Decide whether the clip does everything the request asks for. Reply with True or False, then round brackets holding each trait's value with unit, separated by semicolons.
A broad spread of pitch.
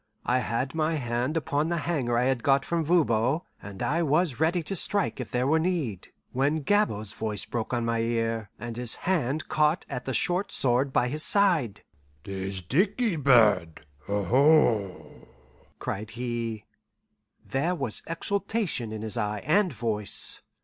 True (6.0 semitones)